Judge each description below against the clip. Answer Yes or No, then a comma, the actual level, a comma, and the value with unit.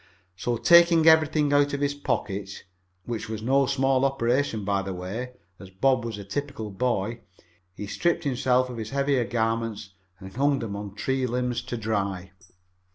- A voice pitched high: No, low, 120 Hz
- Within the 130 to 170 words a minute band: Yes, average, 165 wpm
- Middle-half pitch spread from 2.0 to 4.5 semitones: No, average, 5.0 semitones